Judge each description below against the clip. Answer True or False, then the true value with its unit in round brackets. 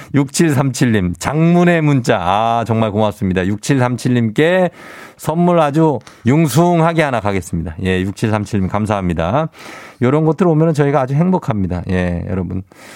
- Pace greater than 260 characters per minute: True (270 characters per minute)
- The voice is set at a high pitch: False (125 Hz)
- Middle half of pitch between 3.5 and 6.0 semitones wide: False (8.1 semitones)